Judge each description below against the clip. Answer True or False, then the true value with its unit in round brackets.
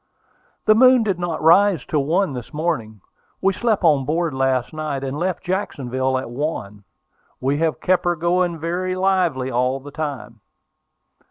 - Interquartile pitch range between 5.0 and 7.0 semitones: True (5.5 semitones)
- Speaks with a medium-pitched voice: True (155 Hz)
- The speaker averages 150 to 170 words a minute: True (160 wpm)